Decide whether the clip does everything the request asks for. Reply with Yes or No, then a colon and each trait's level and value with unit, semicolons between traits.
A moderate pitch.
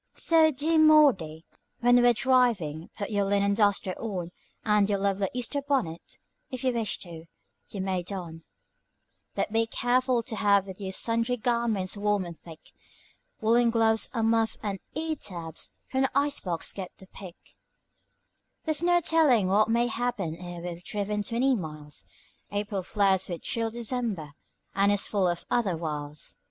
No: high, 210 Hz